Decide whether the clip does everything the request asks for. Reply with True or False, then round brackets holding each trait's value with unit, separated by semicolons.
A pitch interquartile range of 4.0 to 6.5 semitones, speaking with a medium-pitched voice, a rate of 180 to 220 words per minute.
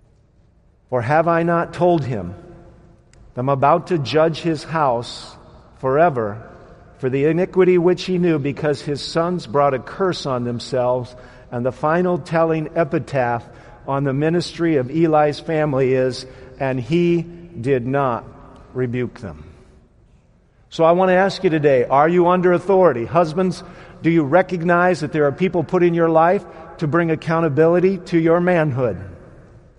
False (4.7 semitones; 160 Hz; 150 wpm)